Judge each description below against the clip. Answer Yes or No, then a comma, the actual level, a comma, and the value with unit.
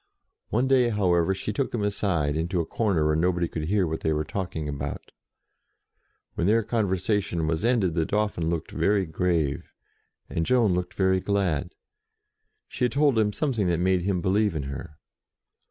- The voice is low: Yes, very low, 95 Hz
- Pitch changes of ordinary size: Yes, average, 4.2 semitones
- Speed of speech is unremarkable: Yes, average, 175 wpm